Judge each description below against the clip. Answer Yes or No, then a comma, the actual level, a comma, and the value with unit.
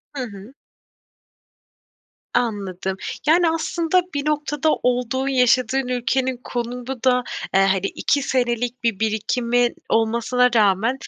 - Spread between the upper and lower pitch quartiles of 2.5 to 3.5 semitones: Yes, average, 2.9 semitones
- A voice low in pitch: No, high, 245 Hz